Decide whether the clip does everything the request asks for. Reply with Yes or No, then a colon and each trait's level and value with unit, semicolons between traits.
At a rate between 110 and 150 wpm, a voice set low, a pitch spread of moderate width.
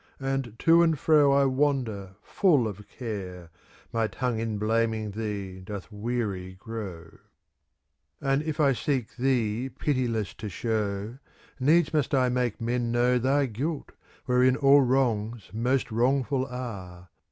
Yes: average, 140 wpm; low, 120 Hz; average, 4.2 semitones